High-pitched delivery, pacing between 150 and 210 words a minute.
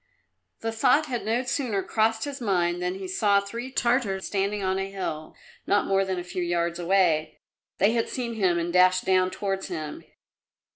Yes: high, 195 Hz; average, 185 wpm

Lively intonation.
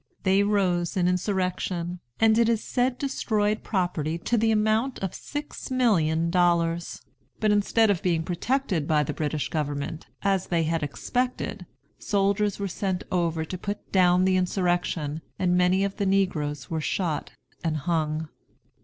No: average, 3.8 semitones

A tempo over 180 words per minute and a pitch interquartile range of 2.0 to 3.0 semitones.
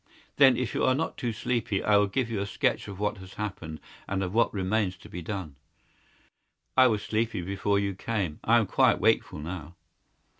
No: average, 200 wpm; average, 3.5 semitones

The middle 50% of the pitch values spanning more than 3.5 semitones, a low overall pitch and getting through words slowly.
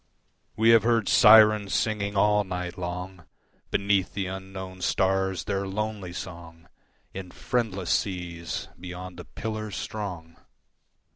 No: narrow, 2.6 semitones; very low, 95 Hz; slow, 120 wpm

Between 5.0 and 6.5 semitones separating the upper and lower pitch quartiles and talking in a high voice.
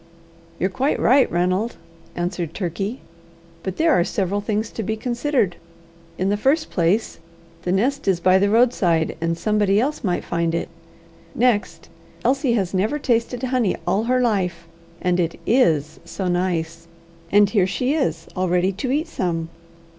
Yes: average, 5.3 semitones; high, 195 Hz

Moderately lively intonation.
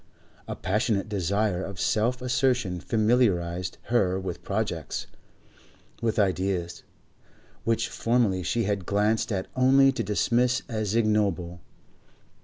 Yes: average, 4.0 semitones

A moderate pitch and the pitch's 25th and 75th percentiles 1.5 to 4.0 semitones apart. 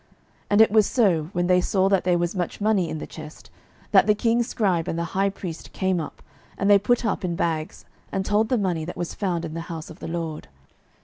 Yes: medium, 180 Hz; average, 3.5 semitones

